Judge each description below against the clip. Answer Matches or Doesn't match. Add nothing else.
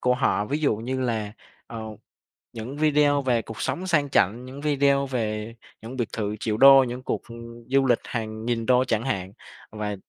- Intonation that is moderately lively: Matches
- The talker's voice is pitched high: Doesn't match